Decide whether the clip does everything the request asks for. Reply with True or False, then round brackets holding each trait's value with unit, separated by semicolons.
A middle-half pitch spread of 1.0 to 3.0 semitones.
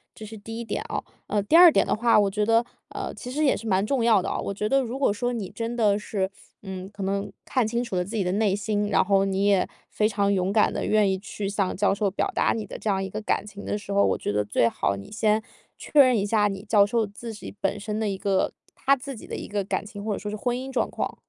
True (2.4 semitones)